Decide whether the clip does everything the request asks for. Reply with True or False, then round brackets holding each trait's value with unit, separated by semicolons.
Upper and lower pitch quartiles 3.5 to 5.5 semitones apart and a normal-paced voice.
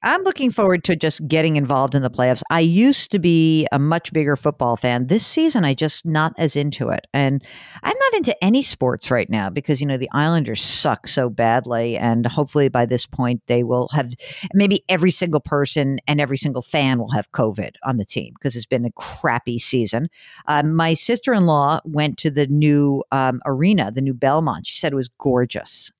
False (4.3 semitones; 210 wpm)